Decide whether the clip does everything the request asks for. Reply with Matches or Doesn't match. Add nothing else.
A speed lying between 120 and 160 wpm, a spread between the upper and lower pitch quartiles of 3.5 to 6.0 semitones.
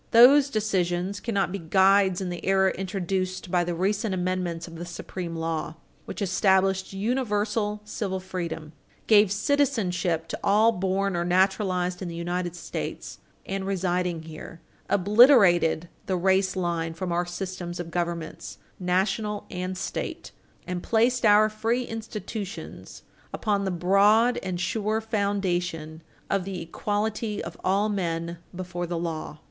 Doesn't match